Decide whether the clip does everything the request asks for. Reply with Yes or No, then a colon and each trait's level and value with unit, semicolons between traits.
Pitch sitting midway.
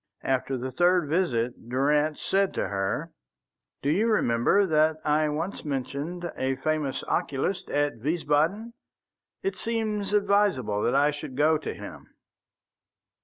Yes: medium, 150 Hz